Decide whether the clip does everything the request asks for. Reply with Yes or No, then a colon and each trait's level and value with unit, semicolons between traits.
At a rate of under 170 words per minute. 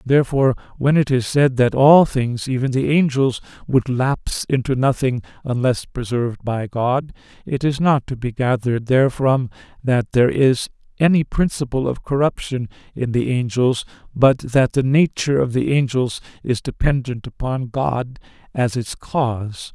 Yes: average, 150 wpm